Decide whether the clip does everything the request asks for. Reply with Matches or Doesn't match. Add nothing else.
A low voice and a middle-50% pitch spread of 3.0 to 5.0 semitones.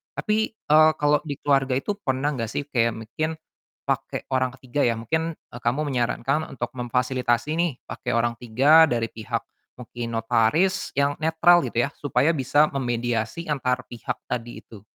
Matches